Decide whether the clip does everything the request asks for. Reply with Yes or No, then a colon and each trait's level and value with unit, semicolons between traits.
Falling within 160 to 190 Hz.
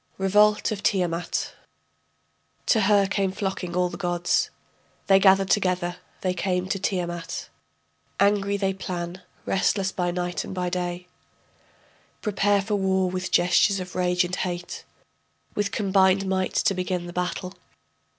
Yes: medium, 185 Hz